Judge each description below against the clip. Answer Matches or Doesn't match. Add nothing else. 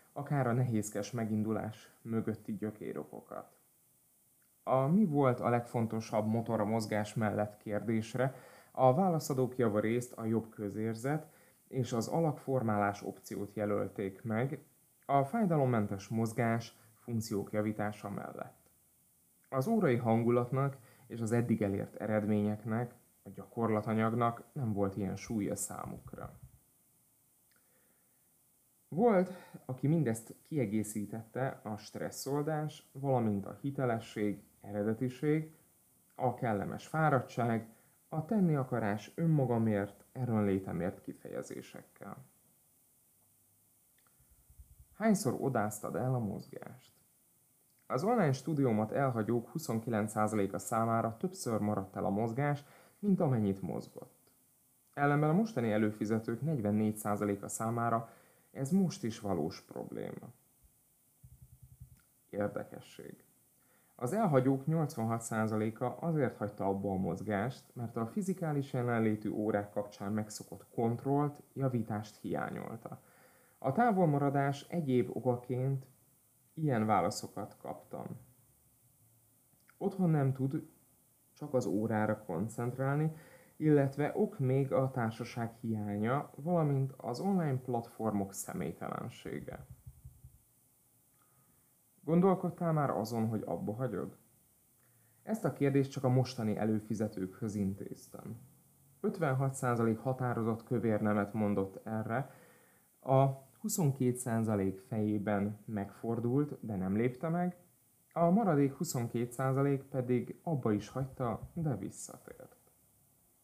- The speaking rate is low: Matches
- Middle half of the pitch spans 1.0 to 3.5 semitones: Doesn't match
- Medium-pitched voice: Doesn't match